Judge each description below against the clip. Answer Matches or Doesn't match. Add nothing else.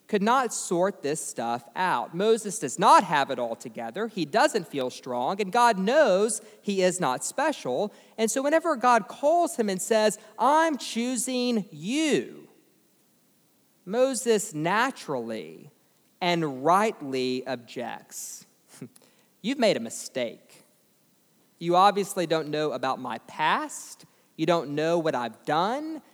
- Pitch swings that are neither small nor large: Doesn't match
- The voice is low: Doesn't match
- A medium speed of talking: Doesn't match